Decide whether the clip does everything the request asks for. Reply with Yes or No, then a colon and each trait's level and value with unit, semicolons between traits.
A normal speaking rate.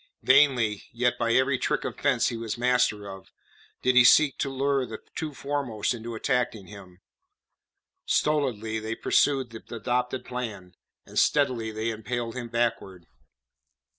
Yes: average, 145 wpm